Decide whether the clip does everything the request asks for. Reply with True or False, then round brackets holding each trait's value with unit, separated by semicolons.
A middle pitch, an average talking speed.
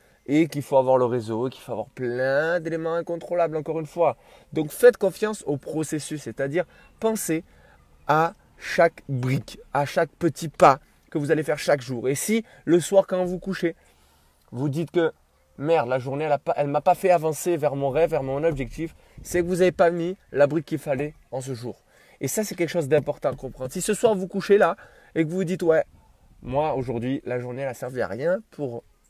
True (155 Hz; 210 wpm)